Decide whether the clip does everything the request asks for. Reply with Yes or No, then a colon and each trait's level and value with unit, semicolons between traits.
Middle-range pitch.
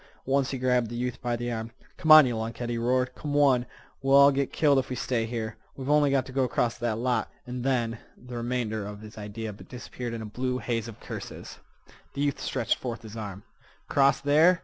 No: low, 125 Hz